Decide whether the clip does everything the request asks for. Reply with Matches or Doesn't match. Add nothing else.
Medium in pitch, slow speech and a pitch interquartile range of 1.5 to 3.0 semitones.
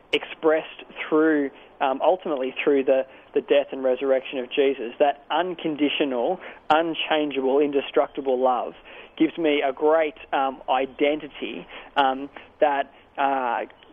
Matches